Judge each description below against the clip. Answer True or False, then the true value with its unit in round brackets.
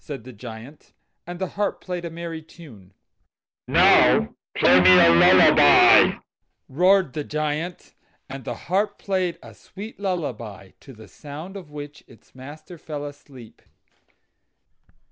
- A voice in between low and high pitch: True (150 Hz)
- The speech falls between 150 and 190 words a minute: False (135 wpm)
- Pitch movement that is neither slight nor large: False (6.3 semitones)